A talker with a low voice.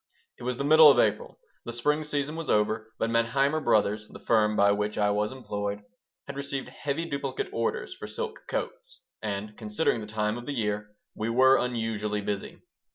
Yes: low, 115 Hz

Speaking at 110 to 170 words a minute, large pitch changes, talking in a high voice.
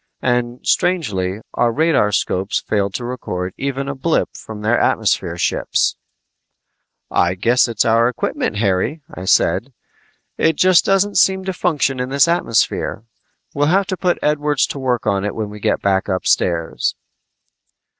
No: average, 150 wpm; wide, 6.8 semitones; low, 125 Hz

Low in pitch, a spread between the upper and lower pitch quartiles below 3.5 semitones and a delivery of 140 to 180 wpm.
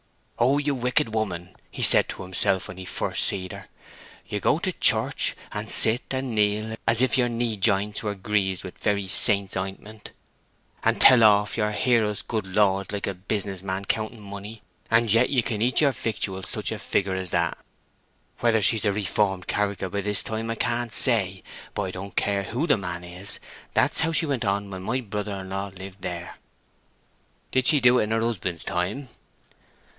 No: low, 105 Hz; average, 3.1 semitones; average, 195 wpm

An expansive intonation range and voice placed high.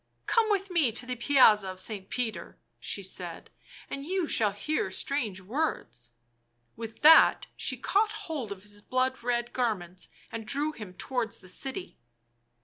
Yes: wide, 6.6 semitones; high, 245 Hz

